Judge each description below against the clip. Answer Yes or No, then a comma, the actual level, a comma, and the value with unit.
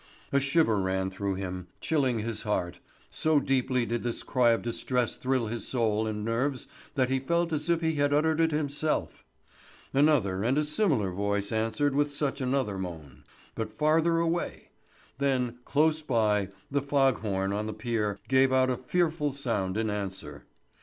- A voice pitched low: Yes, low, 125 Hz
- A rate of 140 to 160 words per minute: No, average, 170 wpm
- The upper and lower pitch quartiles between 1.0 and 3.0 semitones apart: No, wide, 5.4 semitones